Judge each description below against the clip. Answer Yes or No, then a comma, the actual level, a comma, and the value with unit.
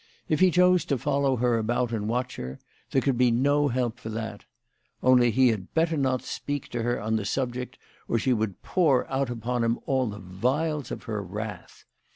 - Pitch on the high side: No, low, 125 Hz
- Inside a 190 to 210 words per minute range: Yes, fast, 205 wpm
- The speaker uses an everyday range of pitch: Yes, average, 3.5 semitones